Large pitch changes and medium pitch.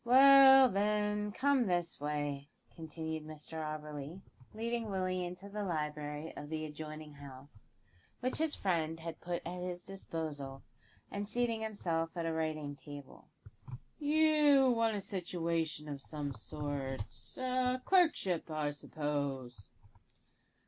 Yes: wide, 5.9 semitones; medium, 165 Hz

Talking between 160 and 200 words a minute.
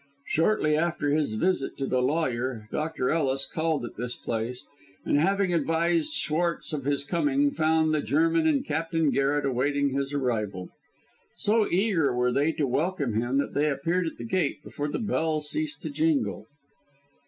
Yes: average, 165 wpm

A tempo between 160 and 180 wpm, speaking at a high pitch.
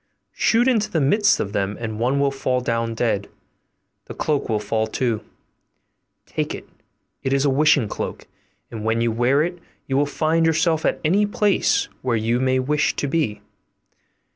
No: average, 175 wpm; low, 135 Hz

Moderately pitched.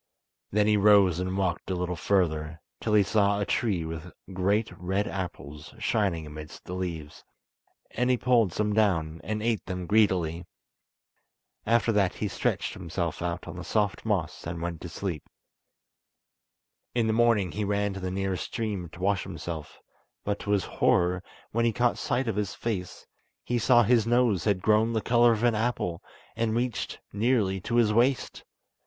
No: low, 100 Hz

